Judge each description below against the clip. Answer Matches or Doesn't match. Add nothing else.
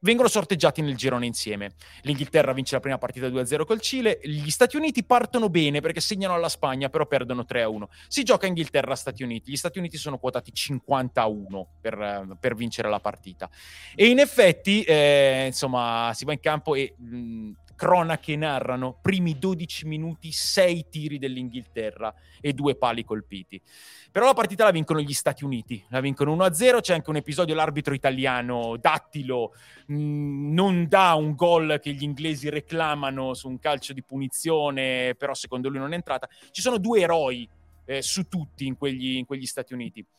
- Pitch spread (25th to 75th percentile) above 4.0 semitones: Matches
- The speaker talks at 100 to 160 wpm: Doesn't match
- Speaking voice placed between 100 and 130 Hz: Doesn't match